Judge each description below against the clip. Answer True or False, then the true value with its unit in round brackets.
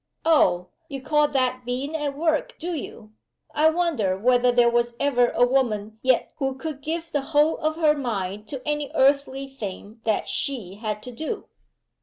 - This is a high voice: True (265 Hz)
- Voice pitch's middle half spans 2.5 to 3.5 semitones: False (4.2 semitones)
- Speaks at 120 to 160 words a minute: False (175 wpm)